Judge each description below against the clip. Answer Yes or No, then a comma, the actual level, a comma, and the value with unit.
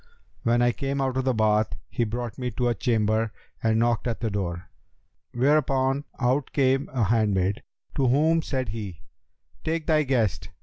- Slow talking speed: No, average, 170 wpm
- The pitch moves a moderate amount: Yes, average, 3.5 semitones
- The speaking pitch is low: Yes, low, 120 Hz